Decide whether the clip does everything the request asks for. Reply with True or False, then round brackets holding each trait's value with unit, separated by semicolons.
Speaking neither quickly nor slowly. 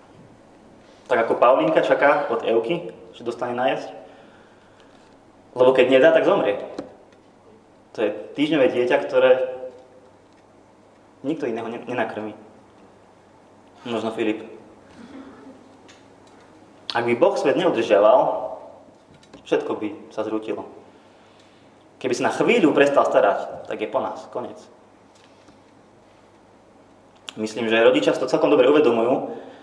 False (105 wpm)